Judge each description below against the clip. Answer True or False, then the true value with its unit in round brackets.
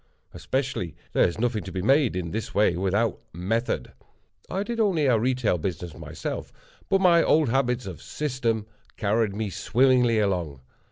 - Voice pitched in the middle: False (115 Hz)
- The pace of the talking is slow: False (160 wpm)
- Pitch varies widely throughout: True (5.7 semitones)